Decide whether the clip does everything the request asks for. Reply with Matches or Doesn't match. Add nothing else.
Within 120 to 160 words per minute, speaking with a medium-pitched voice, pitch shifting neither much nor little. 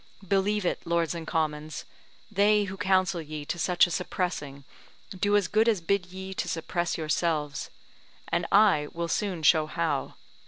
Matches